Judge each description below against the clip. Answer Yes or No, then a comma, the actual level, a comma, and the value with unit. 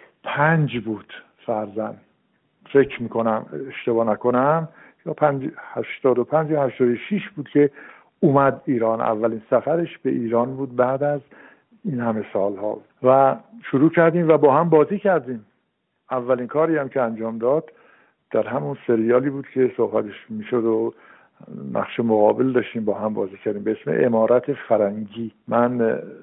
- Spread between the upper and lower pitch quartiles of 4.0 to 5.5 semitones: Yes, average, 4.4 semitones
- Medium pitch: No, low, 125 Hz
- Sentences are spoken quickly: No, average, 145 wpm